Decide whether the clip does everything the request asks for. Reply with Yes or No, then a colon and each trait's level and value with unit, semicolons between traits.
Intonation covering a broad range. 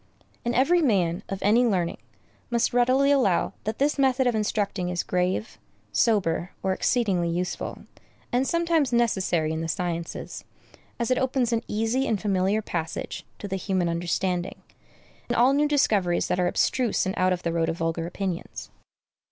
Yes: wide, 5.8 semitones